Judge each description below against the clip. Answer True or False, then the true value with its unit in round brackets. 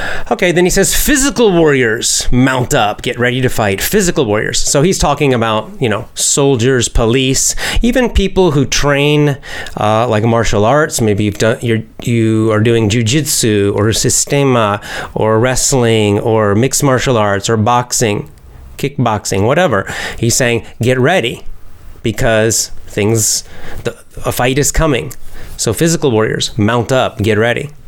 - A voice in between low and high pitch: False (120 Hz)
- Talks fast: False (145 wpm)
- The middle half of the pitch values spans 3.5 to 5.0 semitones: True (4.7 semitones)